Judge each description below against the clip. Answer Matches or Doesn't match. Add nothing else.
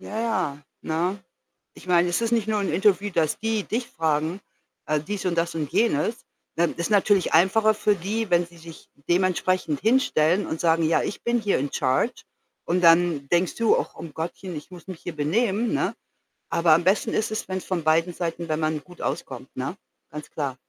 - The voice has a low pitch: Doesn't match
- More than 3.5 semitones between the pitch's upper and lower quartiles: Matches